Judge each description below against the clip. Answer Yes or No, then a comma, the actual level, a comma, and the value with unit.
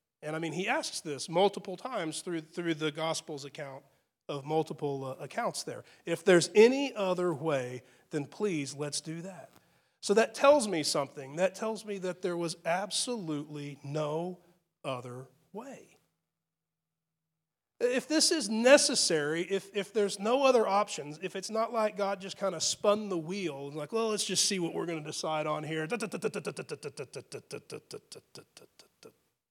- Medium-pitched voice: Yes, medium, 175 Hz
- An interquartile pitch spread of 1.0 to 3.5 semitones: No, average, 5.1 semitones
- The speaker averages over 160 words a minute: No, average, 155 wpm